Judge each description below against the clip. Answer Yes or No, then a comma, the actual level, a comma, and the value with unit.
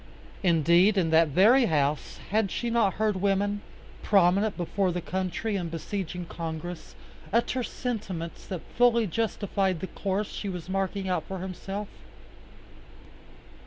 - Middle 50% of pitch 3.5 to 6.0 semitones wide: No, average, 3.1 semitones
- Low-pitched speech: No, high, 190 Hz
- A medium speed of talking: No, slow, 130 wpm